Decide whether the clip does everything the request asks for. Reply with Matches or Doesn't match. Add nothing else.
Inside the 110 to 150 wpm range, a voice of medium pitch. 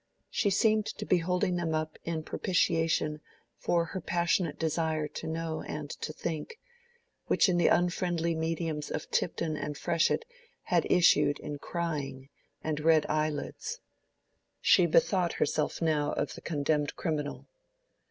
Matches